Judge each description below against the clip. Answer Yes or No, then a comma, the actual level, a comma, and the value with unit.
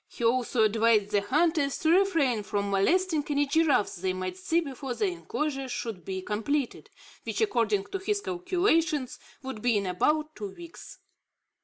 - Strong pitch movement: Yes, wide, 7.8 semitones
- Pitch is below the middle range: No, very high, 265 Hz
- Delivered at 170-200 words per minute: No, average, 160 wpm